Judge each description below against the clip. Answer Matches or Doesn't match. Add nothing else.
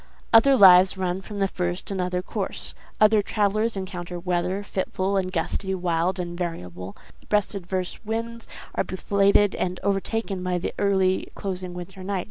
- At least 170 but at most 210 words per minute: Doesn't match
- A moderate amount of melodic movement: Doesn't match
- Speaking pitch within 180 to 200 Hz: Matches